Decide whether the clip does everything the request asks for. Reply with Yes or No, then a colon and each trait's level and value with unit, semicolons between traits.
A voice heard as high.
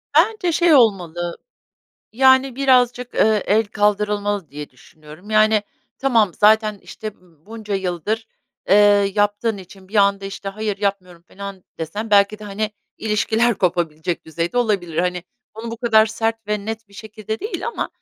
Yes: high, 210 Hz